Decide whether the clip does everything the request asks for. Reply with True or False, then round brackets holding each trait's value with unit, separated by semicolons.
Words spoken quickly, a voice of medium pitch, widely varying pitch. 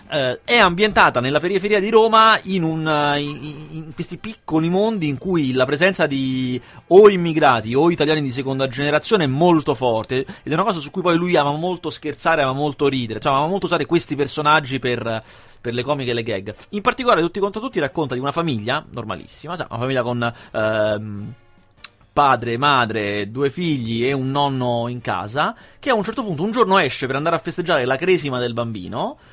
True (195 wpm; 145 Hz; 5.8 semitones)